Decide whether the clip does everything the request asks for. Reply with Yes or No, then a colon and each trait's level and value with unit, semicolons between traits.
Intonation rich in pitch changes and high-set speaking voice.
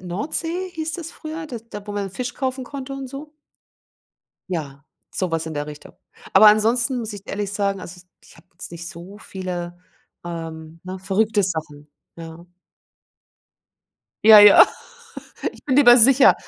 Yes: wide, 6.7 semitones; high, 200 Hz